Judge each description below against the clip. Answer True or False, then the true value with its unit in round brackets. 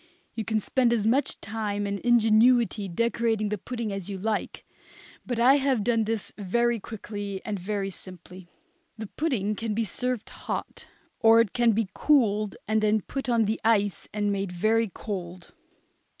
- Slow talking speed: False (165 wpm)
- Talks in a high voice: True (215 Hz)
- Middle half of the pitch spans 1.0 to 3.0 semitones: True (2.5 semitones)